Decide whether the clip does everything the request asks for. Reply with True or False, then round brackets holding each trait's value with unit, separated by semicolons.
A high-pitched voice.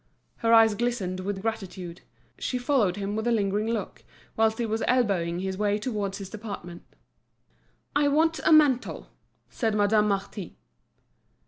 True (210 Hz)